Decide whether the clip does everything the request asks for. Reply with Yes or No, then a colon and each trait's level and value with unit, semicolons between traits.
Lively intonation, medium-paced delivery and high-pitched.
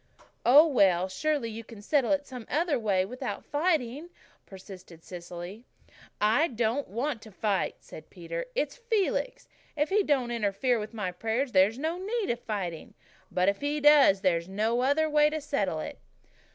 Yes: wide, 7.0 semitones; average, 165 wpm; high, 240 Hz